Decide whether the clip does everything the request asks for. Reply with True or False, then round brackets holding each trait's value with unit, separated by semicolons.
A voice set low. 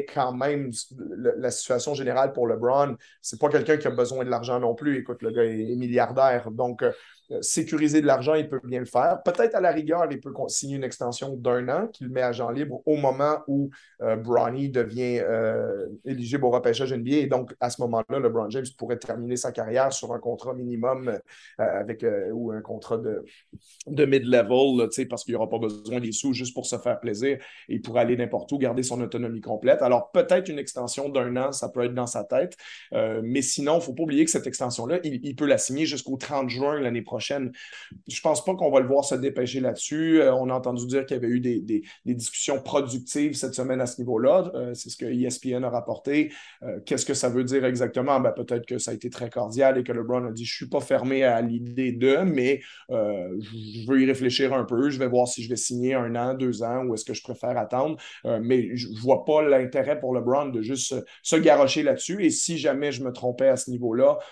True (130 Hz)